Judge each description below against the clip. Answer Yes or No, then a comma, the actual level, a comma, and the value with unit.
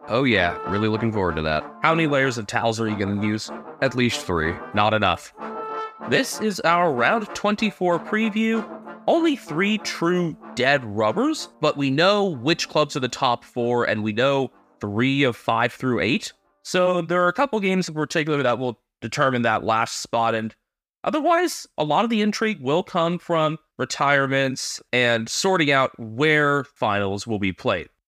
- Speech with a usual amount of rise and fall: No, wide, 7.7 semitones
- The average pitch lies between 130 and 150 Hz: Yes, medium, 140 Hz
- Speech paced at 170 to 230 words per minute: Yes, average, 175 wpm